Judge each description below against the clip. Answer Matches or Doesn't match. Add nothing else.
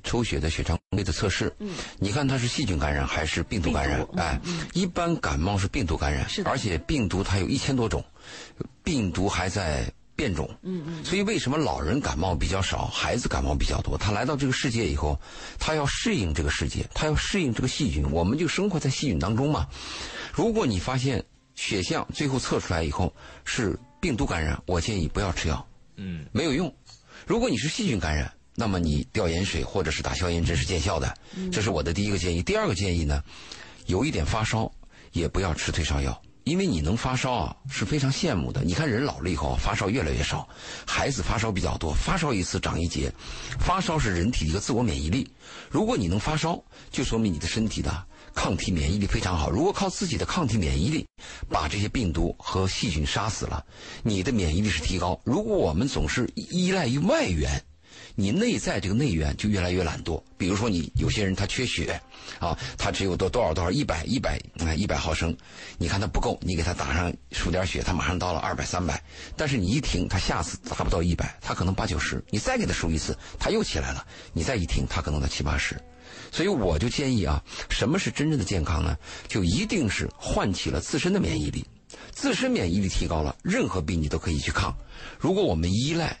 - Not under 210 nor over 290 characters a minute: Doesn't match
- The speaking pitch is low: Matches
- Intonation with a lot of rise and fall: Matches